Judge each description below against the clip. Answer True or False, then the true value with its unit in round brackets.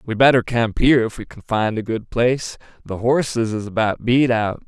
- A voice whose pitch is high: False (115 Hz)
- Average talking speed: False (220 wpm)